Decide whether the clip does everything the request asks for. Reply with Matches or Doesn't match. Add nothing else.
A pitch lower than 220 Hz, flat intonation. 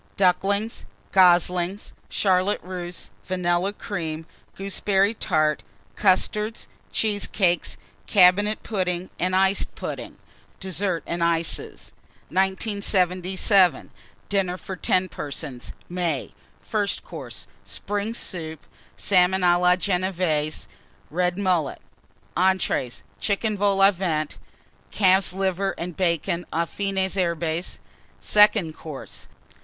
Matches